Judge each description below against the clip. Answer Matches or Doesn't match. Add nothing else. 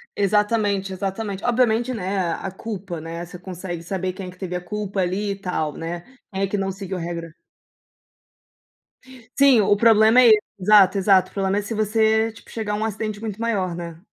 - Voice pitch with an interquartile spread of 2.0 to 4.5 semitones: Matches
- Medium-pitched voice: Doesn't match